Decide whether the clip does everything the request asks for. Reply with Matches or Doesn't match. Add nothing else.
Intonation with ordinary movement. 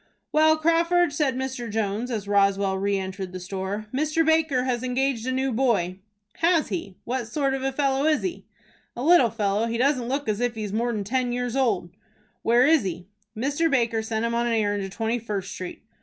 Matches